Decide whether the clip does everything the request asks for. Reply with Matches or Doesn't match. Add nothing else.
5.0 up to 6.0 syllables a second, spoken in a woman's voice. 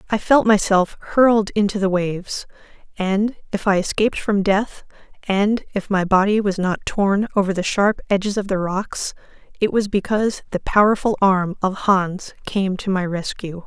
Doesn't match